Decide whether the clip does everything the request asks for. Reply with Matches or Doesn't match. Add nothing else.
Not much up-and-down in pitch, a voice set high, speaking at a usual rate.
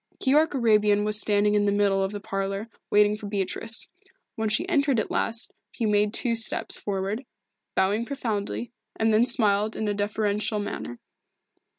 Matches